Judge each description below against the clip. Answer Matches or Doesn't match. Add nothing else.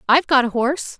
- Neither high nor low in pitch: Doesn't match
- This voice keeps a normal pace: Doesn't match